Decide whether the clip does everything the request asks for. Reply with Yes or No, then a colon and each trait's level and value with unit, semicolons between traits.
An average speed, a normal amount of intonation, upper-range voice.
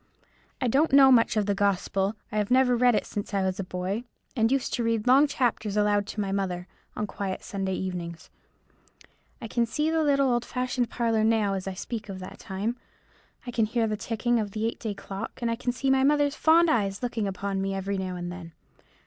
No: fast, 225 wpm; average, 4.1 semitones; high, 215 Hz